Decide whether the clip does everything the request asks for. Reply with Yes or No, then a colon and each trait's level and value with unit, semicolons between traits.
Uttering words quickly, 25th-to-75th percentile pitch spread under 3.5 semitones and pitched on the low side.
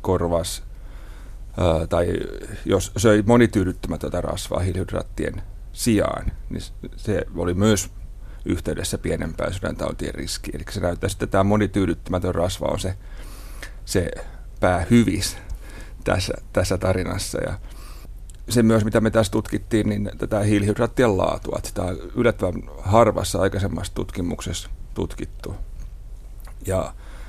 No: average, 110 wpm; average, 3.0 semitones; very low, 95 Hz